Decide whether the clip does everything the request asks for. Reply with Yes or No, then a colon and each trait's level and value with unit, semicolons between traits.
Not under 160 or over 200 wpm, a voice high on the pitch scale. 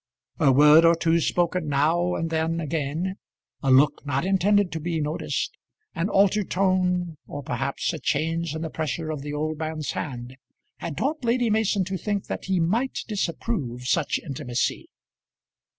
No: average, 165 wpm; medium, 165 Hz